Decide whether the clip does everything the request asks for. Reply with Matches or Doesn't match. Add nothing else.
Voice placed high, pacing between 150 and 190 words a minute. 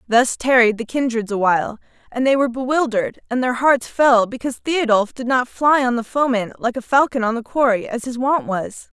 Doesn't match